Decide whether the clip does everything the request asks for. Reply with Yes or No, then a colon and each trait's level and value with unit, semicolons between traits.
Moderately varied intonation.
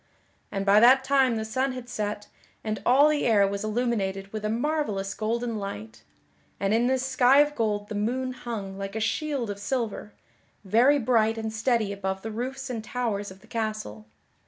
Yes: average, 3.8 semitones